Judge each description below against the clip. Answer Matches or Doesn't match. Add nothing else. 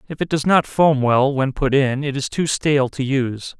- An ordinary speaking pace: Doesn't match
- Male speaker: Matches